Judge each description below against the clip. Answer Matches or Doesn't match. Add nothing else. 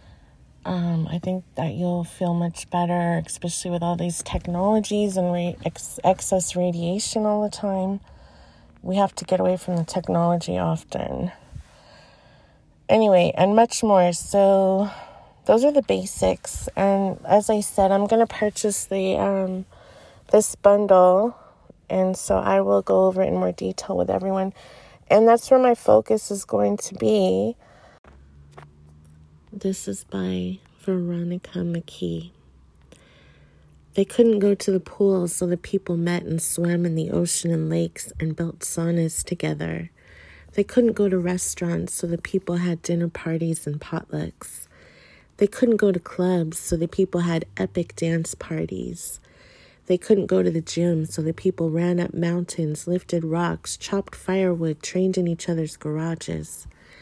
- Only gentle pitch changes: Doesn't match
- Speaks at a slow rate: Doesn't match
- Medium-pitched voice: Matches